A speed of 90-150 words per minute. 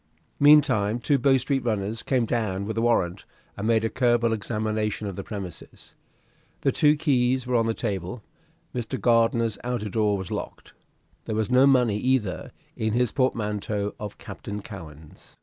No: average, 165 wpm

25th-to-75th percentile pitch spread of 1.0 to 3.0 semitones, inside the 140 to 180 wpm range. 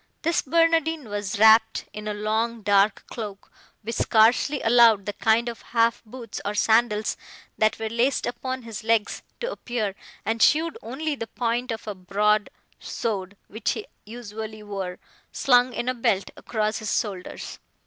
Yes: narrow, 2.4 semitones; average, 160 wpm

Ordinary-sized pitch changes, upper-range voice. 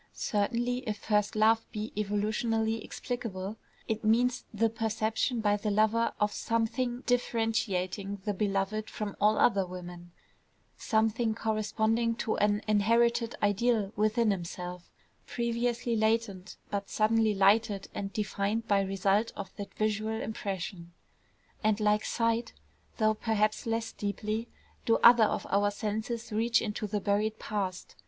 No: narrow, 1.9 semitones; high, 215 Hz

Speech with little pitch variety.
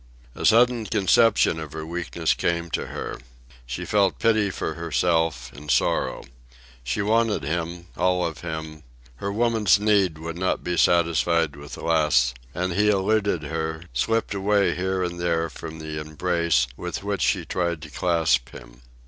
No: average, 3.9 semitones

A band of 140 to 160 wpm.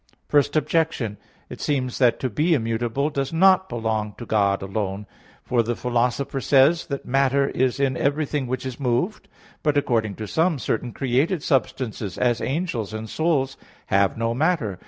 No: average, 170 wpm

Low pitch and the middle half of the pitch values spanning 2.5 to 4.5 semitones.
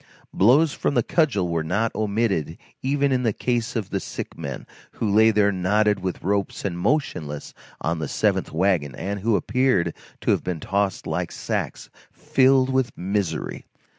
No: low, 100 Hz; average, 5.2 semitones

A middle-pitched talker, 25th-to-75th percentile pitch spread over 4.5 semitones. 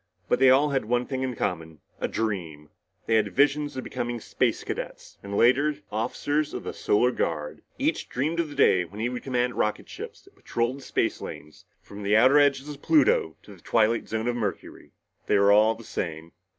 No: low, 120 Hz; average, 5.0 semitones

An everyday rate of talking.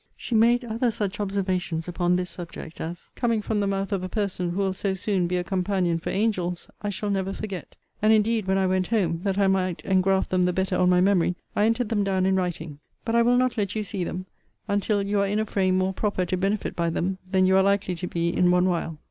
No: fast, 250 wpm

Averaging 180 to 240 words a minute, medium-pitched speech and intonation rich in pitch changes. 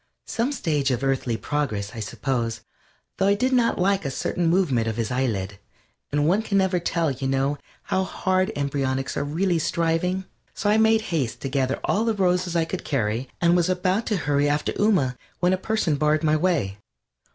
Yes: average, 195 wpm; medium, 160 Hz; wide, 5.8 semitones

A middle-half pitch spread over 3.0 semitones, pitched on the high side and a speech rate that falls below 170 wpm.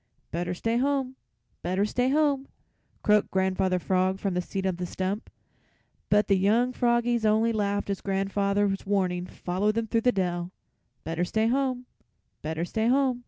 Yes: average, 4.2 semitones; high, 205 Hz; average, 160 wpm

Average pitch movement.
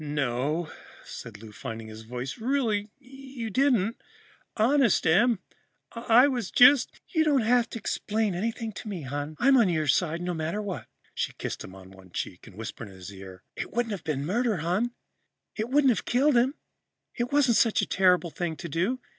No: wide, 8.8 semitones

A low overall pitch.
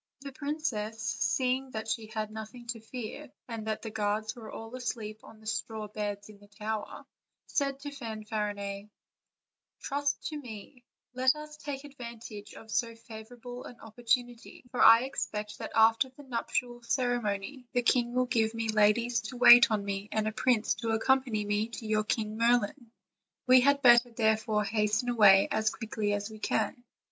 No: high, 225 Hz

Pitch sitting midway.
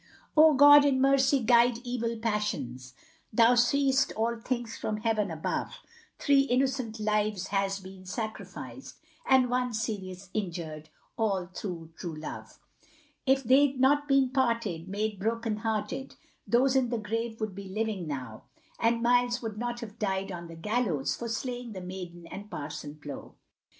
No: high, 220 Hz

